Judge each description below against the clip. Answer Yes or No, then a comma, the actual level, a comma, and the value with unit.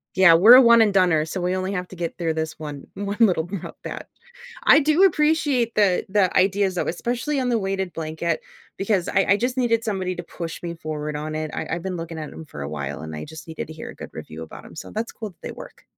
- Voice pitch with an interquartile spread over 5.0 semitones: Yes, wide, 5.5 semitones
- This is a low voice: No, medium, 185 Hz